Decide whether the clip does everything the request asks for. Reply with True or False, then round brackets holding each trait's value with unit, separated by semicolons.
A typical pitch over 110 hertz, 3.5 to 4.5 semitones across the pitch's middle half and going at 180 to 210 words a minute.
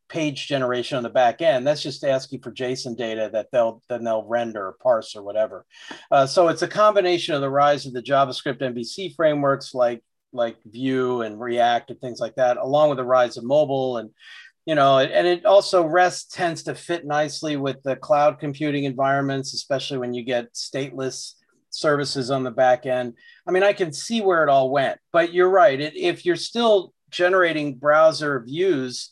True (140 Hz; 4.1 semitones; 190 wpm)